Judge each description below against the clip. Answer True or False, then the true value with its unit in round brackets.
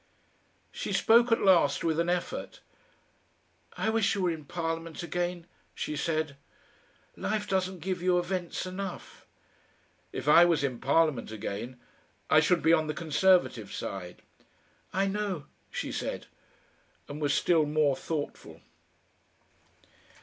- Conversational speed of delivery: False (130 wpm)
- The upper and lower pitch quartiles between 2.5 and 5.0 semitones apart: True (3.7 semitones)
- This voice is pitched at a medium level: True (165 Hz)